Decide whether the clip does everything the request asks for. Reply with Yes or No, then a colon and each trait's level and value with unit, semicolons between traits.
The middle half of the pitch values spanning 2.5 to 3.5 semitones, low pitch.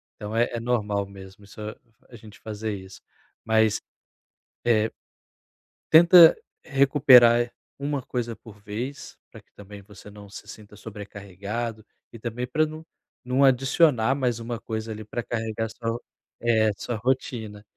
Yes: average, 2.9 semitones; low, 115 Hz